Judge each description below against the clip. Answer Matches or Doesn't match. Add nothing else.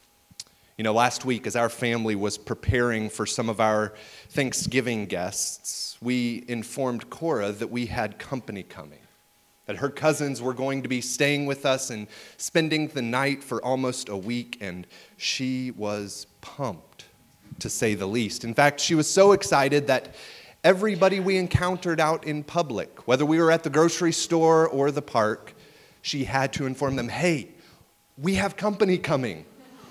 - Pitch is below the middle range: Matches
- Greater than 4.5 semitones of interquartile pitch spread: Matches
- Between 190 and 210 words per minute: Doesn't match